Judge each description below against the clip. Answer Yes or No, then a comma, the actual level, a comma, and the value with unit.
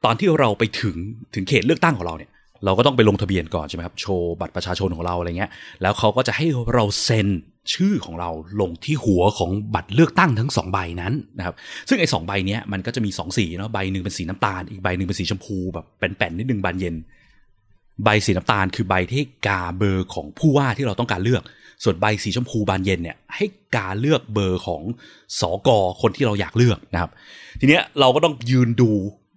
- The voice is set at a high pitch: No, low, 105 Hz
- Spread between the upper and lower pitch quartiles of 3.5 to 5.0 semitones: Yes, average, 4.3 semitones